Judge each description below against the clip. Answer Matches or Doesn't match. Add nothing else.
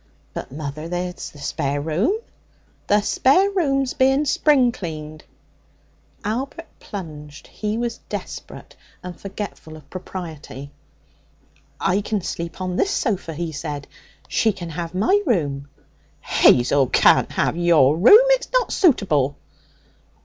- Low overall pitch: Doesn't match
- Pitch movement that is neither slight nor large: Doesn't match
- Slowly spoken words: Matches